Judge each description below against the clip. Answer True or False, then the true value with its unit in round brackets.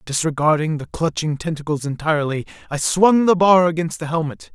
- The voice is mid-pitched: True (160 Hz)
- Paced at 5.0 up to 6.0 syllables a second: True (5.5 syllables/s)